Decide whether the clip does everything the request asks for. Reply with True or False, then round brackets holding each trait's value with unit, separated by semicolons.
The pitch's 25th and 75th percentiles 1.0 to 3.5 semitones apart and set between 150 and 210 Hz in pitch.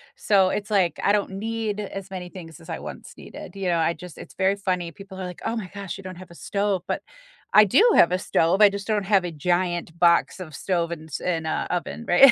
True (2.6 semitones; 185 Hz)